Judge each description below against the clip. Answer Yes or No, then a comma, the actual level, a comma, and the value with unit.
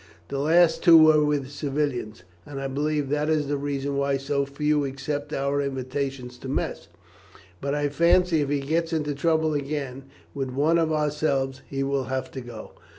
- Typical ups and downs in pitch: No, narrow, 1.8 semitones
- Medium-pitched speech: Yes, medium, 145 Hz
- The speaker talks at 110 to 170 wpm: No, average, 180 wpm